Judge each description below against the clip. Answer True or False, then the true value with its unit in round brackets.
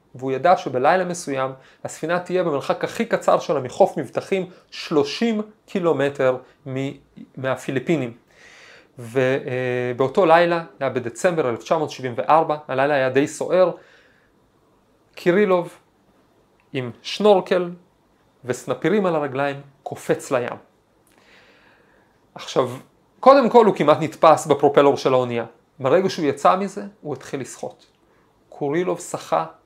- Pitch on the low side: False (150 Hz)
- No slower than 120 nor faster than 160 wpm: False (105 wpm)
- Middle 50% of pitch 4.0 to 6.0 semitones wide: True (5.5 semitones)